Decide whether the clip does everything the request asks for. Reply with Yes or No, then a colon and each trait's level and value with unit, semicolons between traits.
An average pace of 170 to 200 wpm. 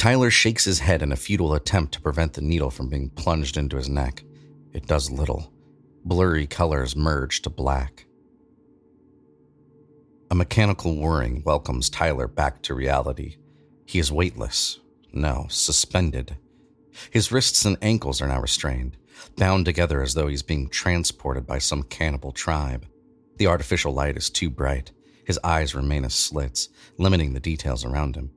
No: average, 155 wpm